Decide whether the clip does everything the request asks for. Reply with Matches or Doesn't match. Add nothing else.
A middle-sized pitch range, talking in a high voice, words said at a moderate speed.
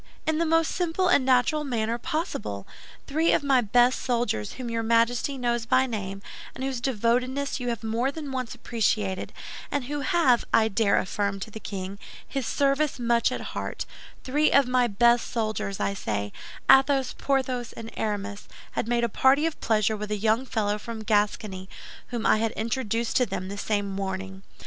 Matches